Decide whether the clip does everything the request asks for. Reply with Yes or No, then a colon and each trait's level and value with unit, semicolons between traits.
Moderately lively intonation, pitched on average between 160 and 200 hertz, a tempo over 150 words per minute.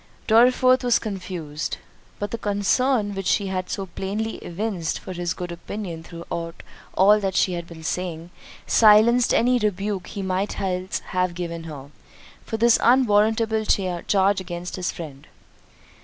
No: average, 3.6 semitones; high, 190 Hz; average, 140 wpm